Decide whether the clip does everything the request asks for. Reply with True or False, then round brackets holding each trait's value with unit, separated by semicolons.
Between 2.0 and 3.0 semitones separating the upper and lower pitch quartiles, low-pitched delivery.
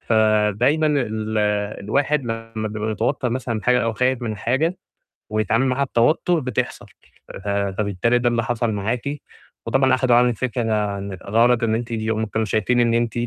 True (2.6 semitones; 115 Hz)